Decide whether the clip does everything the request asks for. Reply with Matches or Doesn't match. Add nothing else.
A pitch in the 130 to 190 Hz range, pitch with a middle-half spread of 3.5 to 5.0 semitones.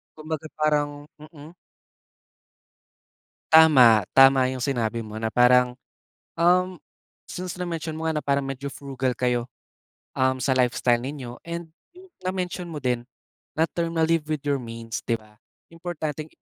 Matches